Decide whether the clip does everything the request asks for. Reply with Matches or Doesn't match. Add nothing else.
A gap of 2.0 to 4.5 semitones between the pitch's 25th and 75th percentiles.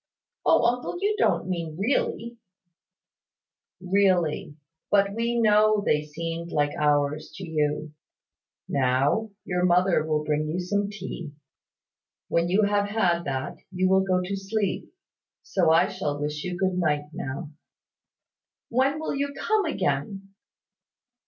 Doesn't match